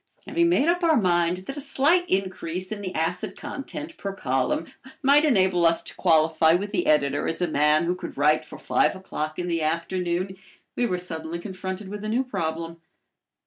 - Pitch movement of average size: Yes, average, 4.7 semitones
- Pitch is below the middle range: No, medium, 180 Hz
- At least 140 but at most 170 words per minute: No, average, 190 wpm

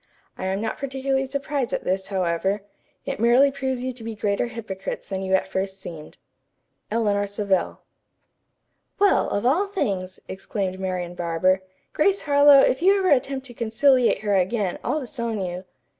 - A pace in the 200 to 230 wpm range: No, average, 160 wpm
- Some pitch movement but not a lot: No, wide, 5.9 semitones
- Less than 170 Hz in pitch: No, high, 220 Hz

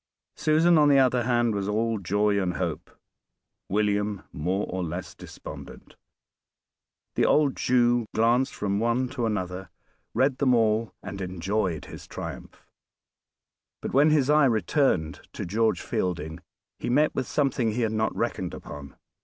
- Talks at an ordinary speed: Yes, average, 145 wpm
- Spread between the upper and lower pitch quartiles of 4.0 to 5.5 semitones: Yes, average, 5.0 semitones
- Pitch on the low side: Yes, low, 110 Hz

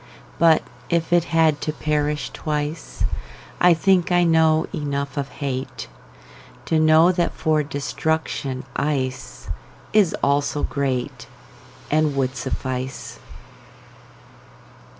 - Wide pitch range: No, average, 3.2 semitones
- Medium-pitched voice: Yes, medium, 150 Hz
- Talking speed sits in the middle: No, slow, 90 wpm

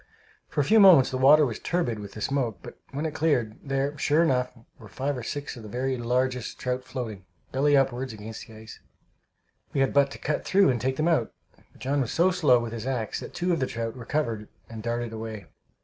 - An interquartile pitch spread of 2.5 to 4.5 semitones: Yes, average, 3.9 semitones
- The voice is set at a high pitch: No, low, 130 Hz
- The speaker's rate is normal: No, fast, 225 wpm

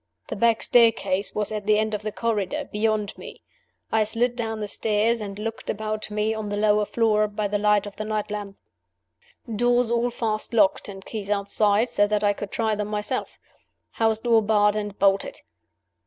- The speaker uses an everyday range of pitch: No, narrow, 1.3 semitones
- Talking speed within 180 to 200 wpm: Yes, average, 190 wpm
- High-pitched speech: Yes, high, 215 Hz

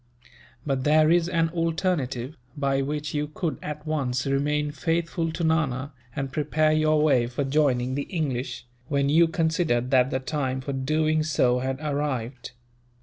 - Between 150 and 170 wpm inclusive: Yes, average, 155 wpm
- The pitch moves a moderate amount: Yes, average, 3.0 semitones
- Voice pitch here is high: No, medium, 145 Hz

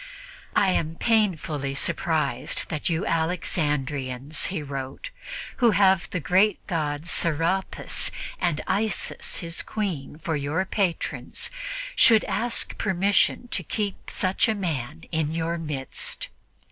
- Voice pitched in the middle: Yes, medium, 165 Hz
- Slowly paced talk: Yes, slow, 120 wpm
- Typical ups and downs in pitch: Yes, average, 4.5 semitones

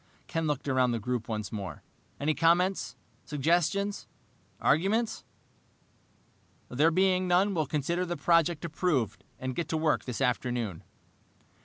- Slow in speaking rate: Yes, slow, 130 wpm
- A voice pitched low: No, medium, 155 Hz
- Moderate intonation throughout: No, wide, 5.8 semitones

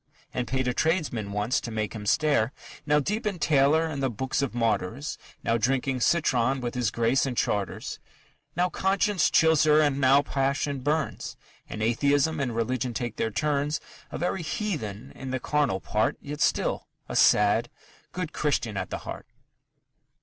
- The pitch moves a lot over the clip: No, average, 4.4 semitones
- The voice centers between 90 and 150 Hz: Yes, low, 135 Hz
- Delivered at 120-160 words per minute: No, average, 170 wpm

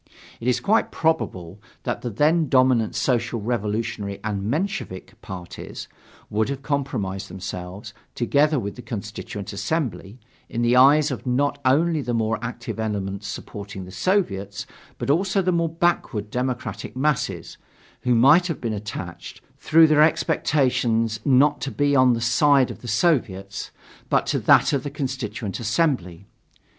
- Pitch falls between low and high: No, low, 120 Hz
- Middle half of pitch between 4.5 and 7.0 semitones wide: Yes, wide, 5.6 semitones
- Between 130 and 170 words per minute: Yes, average, 145 wpm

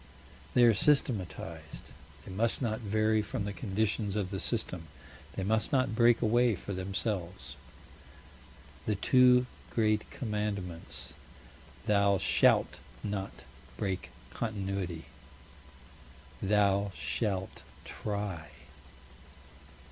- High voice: No, low, 100 Hz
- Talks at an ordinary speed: No, slow, 95 wpm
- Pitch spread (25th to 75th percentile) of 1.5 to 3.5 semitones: Yes, average, 2.7 semitones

